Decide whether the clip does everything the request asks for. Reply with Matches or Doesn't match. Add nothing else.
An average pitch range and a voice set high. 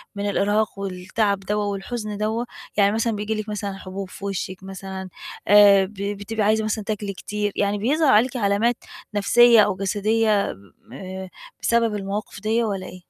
Doesn't match